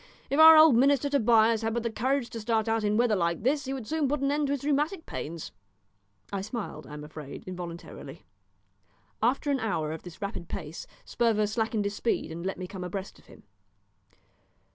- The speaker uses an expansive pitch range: Yes, wide, 6.4 semitones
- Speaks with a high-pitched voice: Yes, high, 225 Hz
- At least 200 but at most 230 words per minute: Yes, fast, 205 wpm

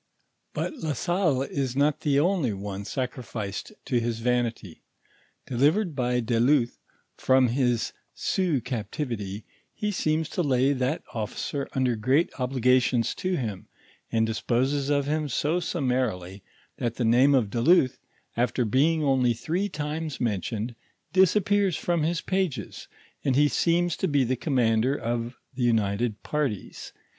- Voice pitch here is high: No, low, 130 Hz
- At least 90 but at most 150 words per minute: Yes, average, 145 wpm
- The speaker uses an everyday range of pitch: Yes, average, 4.5 semitones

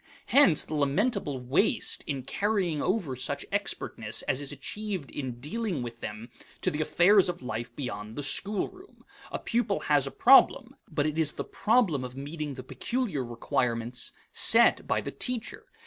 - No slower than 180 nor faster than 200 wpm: No, average, 165 wpm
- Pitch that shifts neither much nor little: No, wide, 7.8 semitones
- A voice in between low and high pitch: Yes, medium, 150 Hz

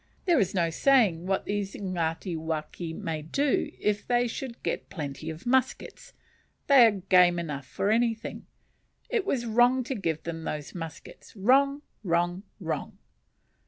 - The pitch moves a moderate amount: No, wide, 6.7 semitones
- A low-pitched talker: No, high, 195 Hz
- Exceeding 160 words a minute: No, average, 145 wpm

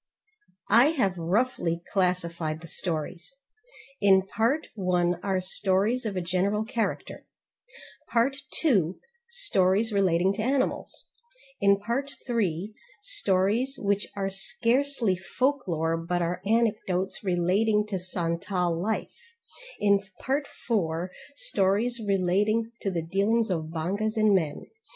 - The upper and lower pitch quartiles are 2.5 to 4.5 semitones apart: Yes, average, 4.1 semitones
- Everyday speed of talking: No, slow, 115 wpm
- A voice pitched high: Yes, high, 195 Hz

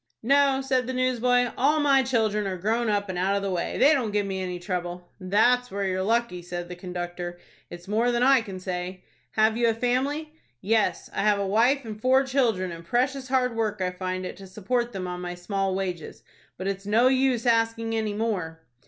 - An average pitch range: Yes, average, 5.0 semitones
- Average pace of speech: No, fast, 215 wpm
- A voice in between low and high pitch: No, high, 215 Hz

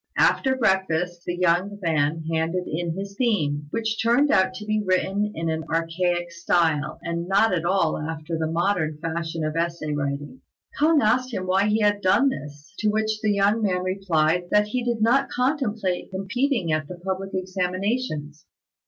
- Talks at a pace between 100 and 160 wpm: No, average, 170 wpm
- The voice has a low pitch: No, medium, 185 Hz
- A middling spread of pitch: Yes, average, 4.4 semitones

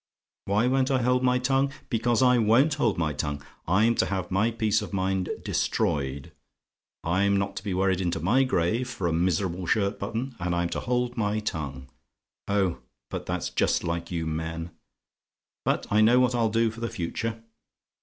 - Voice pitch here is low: Yes, low, 100 Hz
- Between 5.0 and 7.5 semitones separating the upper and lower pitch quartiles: Yes, wide, 5.5 semitones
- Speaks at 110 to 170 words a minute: No, average, 180 wpm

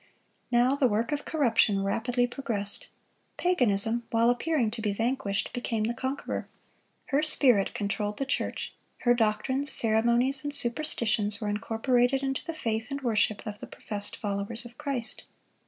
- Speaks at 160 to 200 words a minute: No, average, 150 wpm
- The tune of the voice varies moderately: Yes, average, 3.8 semitones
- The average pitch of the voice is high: Yes, high, 235 Hz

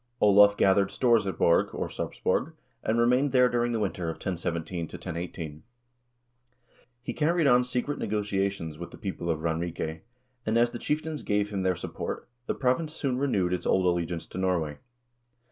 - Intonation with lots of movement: Yes, wide, 6.1 semitones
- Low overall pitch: Yes, low, 100 Hz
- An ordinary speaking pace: Yes, average, 165 wpm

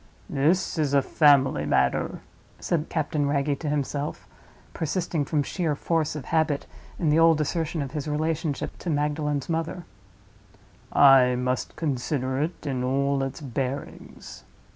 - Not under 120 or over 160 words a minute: Yes, average, 140 wpm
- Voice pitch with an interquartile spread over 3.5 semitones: No, narrow, 2.6 semitones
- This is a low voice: No, medium, 145 Hz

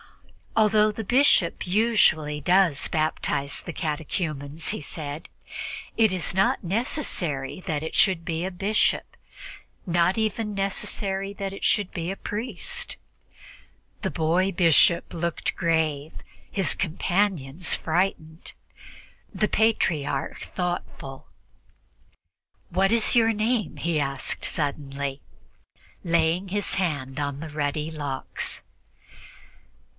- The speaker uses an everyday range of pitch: Yes, average, 4.5 semitones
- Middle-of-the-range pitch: Yes, medium, 170 Hz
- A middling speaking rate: No, slow, 110 wpm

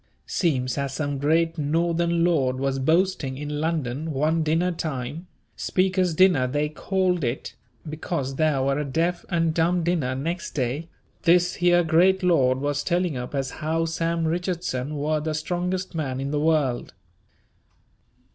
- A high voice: No, medium, 160 Hz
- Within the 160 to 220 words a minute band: No, average, 150 wpm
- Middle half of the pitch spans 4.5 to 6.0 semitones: No, average, 3.7 semitones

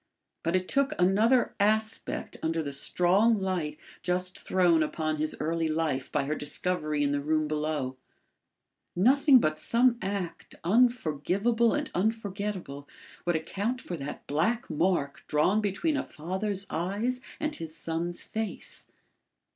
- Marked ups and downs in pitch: Yes, wide, 5.8 semitones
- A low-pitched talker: No, medium, 180 Hz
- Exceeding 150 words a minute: No, slow, 135 wpm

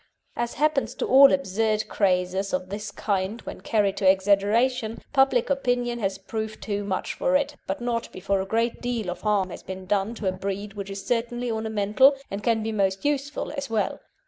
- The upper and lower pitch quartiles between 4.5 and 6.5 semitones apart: No, average, 3.5 semitones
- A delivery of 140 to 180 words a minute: No, average, 195 wpm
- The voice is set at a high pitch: Yes, high, 215 Hz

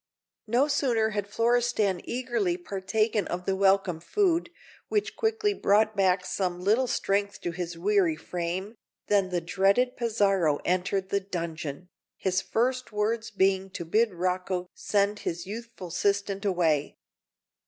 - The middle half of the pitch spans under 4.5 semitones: Yes, average, 3.5 semitones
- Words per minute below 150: Yes, slow, 135 wpm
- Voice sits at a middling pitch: No, high, 195 Hz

